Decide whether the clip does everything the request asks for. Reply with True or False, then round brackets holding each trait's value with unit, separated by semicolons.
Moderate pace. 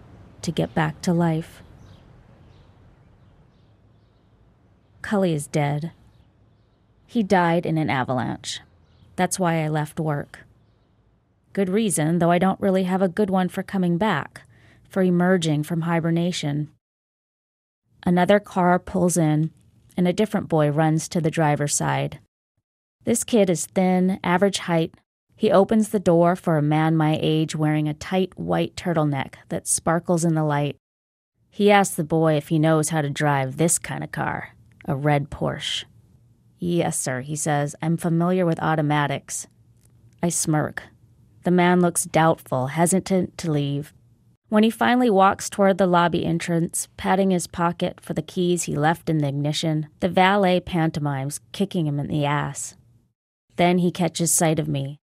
True (150 wpm)